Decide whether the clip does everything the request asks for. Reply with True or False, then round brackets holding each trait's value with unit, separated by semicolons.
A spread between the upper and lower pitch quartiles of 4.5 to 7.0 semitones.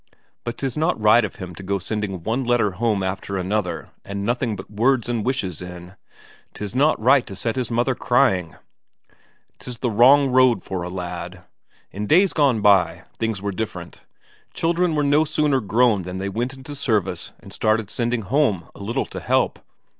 True (5.0 semitones)